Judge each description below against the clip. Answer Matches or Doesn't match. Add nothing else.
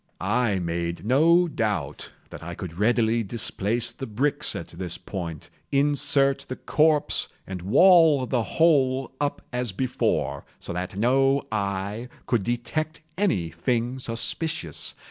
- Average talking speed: Doesn't match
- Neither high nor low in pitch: Doesn't match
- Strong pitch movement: Matches